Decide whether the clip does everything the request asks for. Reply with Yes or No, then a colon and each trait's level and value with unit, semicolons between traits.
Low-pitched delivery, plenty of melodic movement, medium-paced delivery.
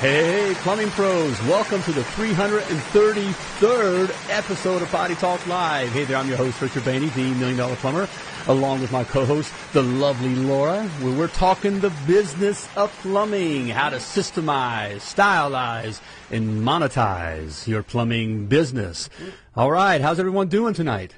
No: medium, 155 Hz; wide, 7.3 semitones; average, 145 wpm